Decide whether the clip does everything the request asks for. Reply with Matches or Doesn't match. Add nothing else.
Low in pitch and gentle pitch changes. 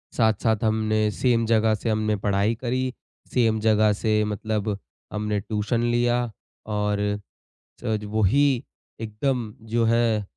Matches